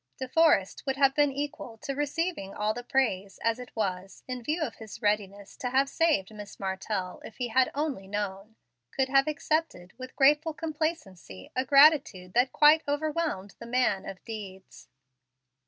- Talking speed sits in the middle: Yes, average, 170 wpm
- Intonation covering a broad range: Yes, wide, 6.5 semitones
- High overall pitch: Yes, very high, 250 Hz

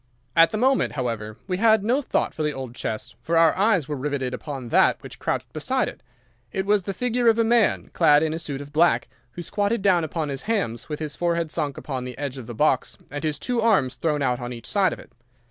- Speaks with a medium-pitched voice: Yes, medium, 155 Hz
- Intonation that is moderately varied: No, wide, 6.7 semitones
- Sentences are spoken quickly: Yes, fast, 245 wpm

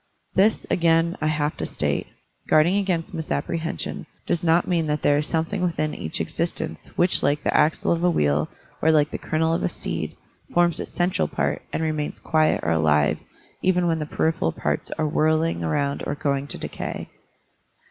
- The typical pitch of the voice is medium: Yes, medium, 155 Hz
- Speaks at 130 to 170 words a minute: No, average, 180 wpm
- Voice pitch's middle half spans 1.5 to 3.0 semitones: Yes, average, 2.7 semitones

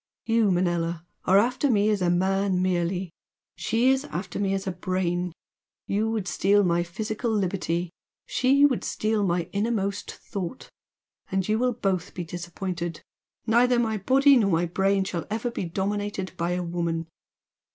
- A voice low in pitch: No, high, 195 Hz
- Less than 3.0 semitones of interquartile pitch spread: No, average, 3.7 semitones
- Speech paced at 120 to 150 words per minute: No, average, 160 wpm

